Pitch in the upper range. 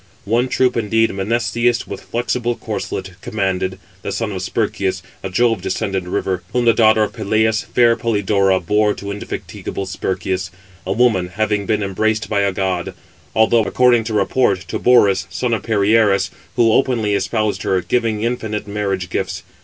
No: low, 105 Hz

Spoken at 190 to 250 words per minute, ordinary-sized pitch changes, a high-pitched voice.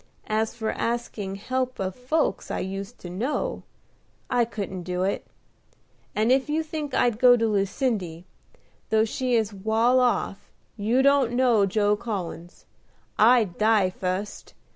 No: average, 140 wpm; average, 4.1 semitones; high, 220 Hz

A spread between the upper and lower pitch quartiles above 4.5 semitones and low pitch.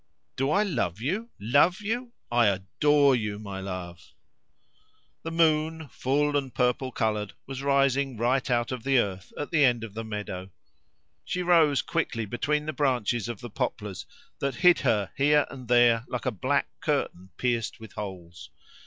Yes: wide, 5.4 semitones; low, 125 Hz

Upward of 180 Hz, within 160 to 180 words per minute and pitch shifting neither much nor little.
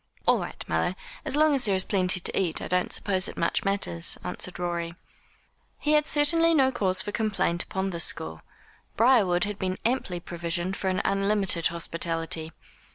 Yes: high, 190 Hz; average, 175 wpm; average, 3.8 semitones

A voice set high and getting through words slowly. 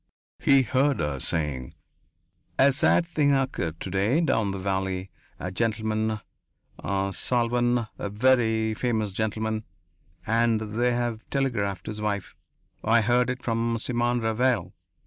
No: low, 110 Hz; slow, 125 wpm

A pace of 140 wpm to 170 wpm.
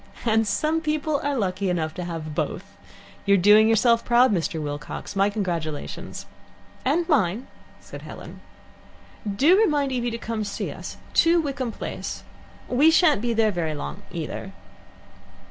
Yes: average, 150 wpm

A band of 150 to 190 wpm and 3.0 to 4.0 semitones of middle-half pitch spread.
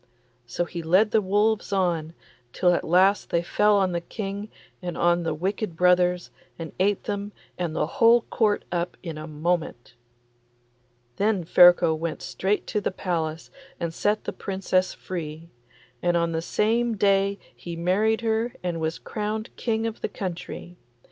Yes: average, 160 wpm; average, 3.5 semitones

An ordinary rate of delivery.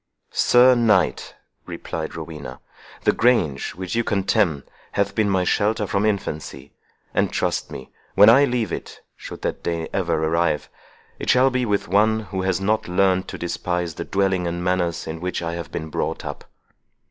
Yes: average, 165 wpm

